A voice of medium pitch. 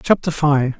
Yes: medium, 150 Hz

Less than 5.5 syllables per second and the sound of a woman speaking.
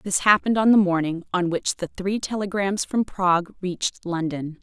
Yes: 5.0 syllables/s; female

